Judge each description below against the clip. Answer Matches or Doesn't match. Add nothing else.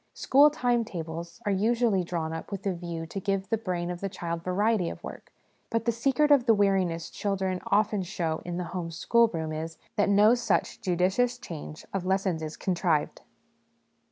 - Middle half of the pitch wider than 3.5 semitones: Matches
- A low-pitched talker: Doesn't match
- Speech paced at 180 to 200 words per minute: Matches